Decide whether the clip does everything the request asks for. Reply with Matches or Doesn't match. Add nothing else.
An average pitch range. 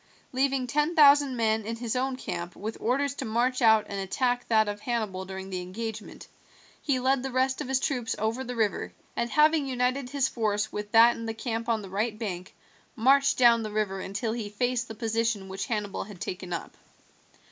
Matches